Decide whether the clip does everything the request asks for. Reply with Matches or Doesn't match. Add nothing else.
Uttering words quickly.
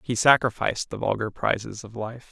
Doesn't match